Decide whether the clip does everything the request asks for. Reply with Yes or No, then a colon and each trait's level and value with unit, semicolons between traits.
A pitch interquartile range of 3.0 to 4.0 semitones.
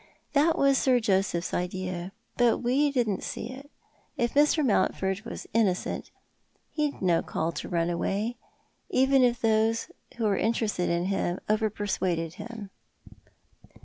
No: average, 4.8 semitones